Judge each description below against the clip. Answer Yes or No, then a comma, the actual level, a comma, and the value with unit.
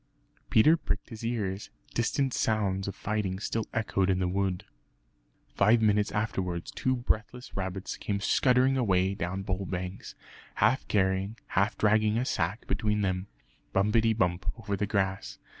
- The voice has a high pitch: No, low, 100 Hz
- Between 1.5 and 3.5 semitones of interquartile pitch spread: Yes, average, 2.9 semitones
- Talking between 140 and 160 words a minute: Yes, average, 145 wpm